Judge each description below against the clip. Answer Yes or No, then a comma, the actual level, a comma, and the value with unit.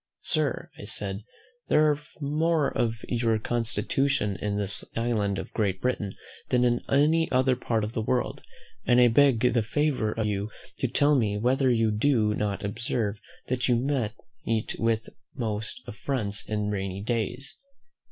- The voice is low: Yes, low, 115 Hz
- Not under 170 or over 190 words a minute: No, average, 155 wpm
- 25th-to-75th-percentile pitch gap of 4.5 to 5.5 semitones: No, average, 3.5 semitones